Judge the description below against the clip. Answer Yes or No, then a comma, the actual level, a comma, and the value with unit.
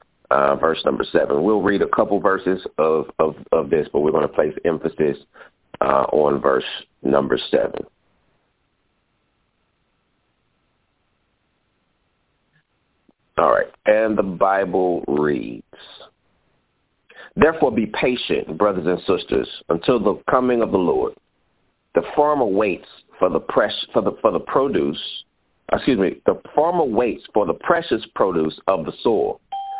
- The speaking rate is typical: No, slow, 130 wpm